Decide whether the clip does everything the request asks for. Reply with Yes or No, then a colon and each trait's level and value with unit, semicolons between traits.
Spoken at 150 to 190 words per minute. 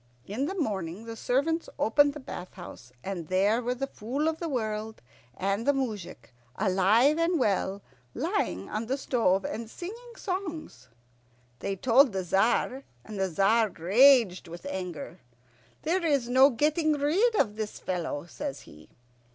Yes: average, 155 wpm